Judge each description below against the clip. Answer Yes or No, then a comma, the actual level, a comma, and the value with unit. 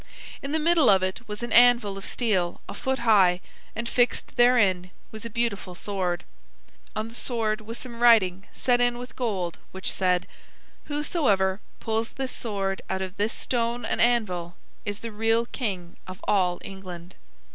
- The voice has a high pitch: Yes, high, 215 Hz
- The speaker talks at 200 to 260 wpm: No, average, 170 wpm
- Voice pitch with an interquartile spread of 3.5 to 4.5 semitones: Yes, average, 4.2 semitones